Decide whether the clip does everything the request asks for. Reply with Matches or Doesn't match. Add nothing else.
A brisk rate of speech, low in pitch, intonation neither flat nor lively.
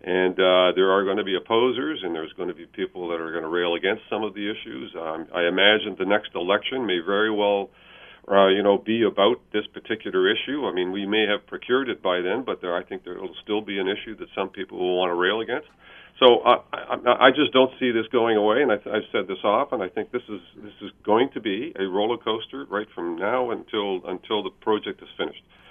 Matches